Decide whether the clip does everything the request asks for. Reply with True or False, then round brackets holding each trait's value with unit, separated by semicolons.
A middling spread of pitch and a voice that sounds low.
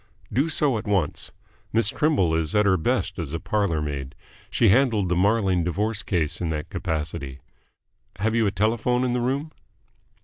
False (5.8 semitones; 100 Hz)